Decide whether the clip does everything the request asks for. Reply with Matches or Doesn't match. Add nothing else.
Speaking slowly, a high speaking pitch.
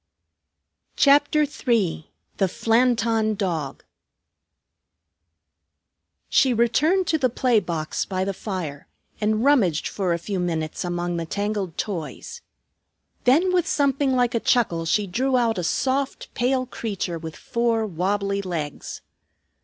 Matches